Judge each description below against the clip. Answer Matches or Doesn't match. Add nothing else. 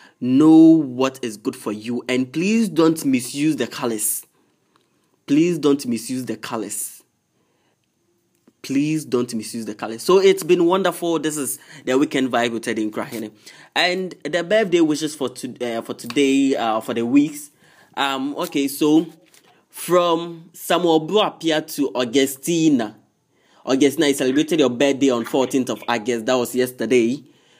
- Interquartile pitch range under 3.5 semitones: Doesn't match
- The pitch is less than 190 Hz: Matches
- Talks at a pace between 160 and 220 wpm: Doesn't match